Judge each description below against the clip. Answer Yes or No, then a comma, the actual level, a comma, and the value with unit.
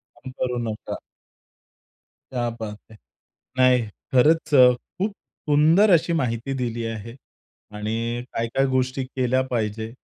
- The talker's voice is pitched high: No, low, 125 Hz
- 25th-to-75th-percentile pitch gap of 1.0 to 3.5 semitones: Yes, average, 2.7 semitones